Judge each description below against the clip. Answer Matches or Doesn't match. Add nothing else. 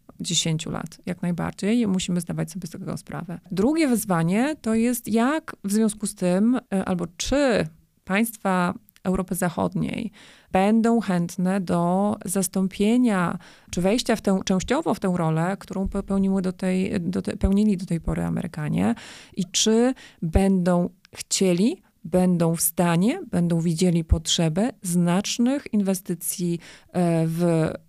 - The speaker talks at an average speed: Matches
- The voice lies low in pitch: Doesn't match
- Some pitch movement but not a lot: Matches